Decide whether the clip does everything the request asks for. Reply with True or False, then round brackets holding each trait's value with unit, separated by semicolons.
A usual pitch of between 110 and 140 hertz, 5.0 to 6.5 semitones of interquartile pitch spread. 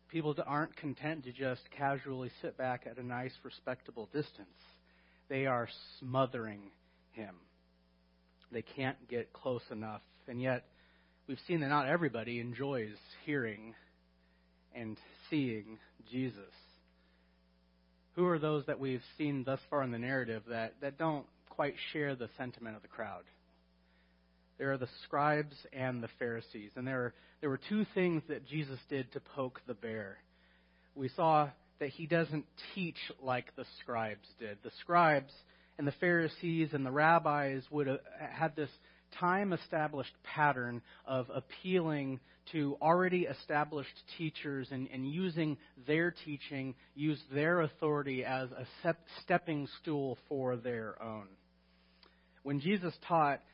True (135 Hz; 5.4 semitones)